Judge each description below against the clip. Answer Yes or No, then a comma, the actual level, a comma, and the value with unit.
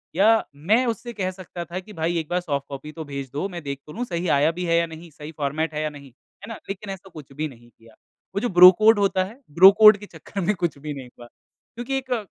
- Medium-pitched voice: Yes, medium, 170 Hz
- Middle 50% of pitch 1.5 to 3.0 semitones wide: No, average, 5.0 semitones